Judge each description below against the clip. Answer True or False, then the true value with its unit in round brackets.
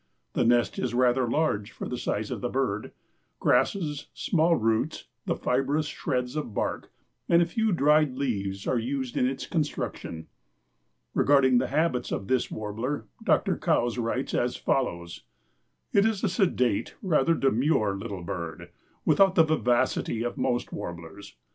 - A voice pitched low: True (125 Hz)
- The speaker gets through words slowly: False (155 wpm)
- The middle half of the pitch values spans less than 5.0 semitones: False (5.4 semitones)